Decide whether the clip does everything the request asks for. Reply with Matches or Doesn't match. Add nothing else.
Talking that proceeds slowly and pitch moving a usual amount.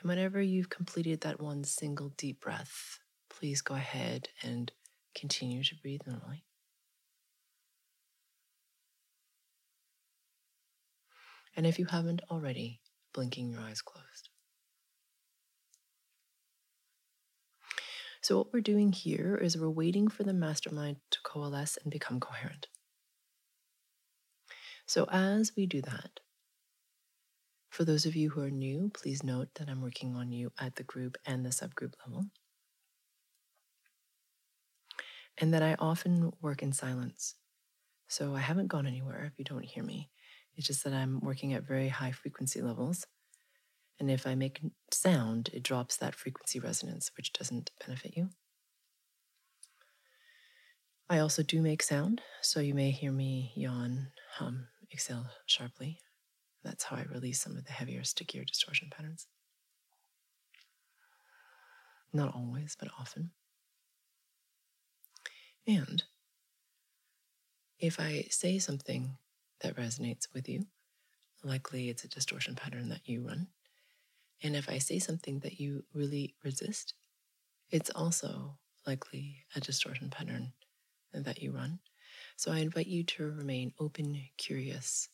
Matches